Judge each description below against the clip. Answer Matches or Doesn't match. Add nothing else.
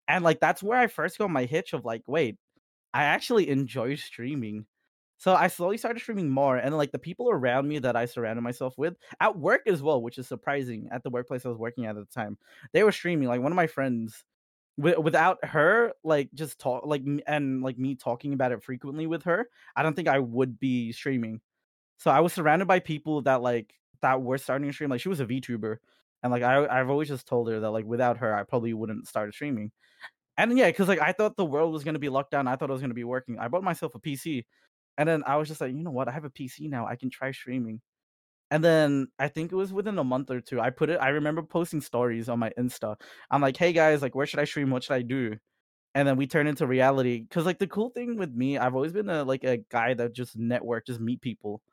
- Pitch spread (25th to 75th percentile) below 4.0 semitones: Doesn't match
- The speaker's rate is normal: Doesn't match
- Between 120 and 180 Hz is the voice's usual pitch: Matches